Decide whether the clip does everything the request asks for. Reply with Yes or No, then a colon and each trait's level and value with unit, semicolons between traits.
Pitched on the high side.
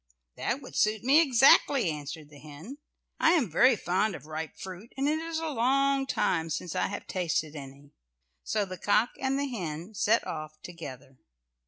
Yes: high, 195 Hz